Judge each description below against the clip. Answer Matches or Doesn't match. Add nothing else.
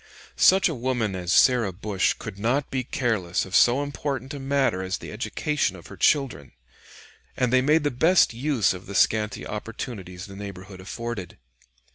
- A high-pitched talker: Doesn't match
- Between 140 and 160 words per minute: Doesn't match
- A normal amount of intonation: Doesn't match